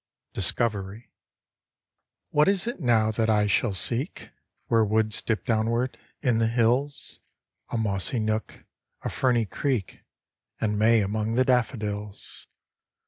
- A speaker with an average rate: No, slow, 125 wpm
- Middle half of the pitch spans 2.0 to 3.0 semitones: Yes, narrow, 2.4 semitones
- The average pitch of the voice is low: Yes, low, 110 Hz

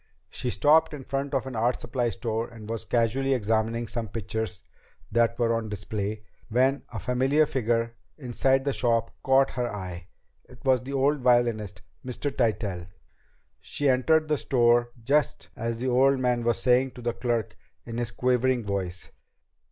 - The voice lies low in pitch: Yes, low, 120 Hz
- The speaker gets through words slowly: No, average, 165 wpm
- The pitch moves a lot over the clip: No, average, 2.7 semitones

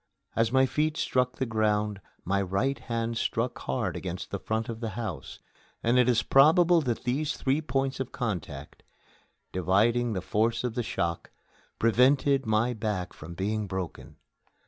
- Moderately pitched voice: No, low, 115 Hz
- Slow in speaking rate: No, average, 160 wpm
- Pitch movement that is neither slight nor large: Yes, average, 3.8 semitones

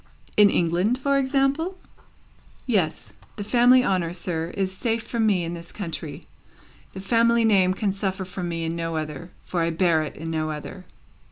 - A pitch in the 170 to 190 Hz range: Yes, medium, 185 Hz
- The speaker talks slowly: No, average, 175 wpm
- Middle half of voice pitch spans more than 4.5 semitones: Yes, average, 5.3 semitones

